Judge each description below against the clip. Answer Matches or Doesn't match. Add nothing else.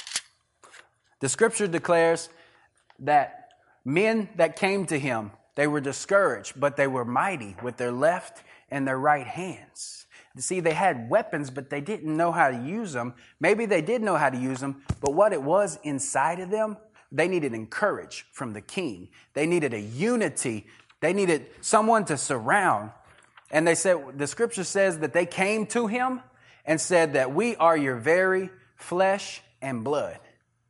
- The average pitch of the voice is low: Doesn't match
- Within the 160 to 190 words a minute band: Matches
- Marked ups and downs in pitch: Matches